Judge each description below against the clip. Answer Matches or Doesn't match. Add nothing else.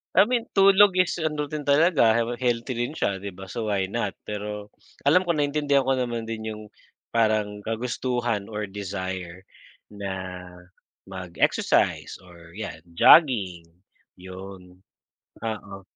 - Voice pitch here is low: Matches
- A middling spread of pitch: Doesn't match